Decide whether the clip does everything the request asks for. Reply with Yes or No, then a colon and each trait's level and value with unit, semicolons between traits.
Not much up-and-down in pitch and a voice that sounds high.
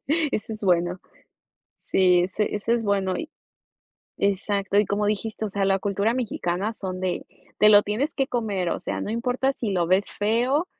No: average, 3.2 semitones; high, 205 Hz